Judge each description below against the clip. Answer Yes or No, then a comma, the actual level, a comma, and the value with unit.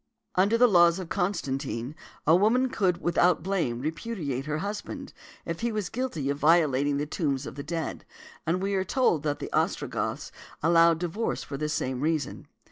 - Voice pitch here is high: No, medium, 165 Hz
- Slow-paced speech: No, average, 180 wpm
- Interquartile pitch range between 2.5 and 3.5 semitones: No, average, 5.0 semitones